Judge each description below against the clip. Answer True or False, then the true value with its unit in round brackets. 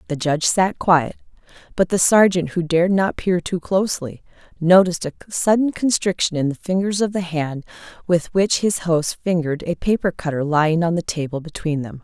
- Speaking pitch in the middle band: True (170 Hz)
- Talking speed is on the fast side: False (185 wpm)